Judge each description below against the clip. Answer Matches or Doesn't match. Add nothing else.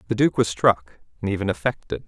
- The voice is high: Doesn't match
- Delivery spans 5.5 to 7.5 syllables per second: Matches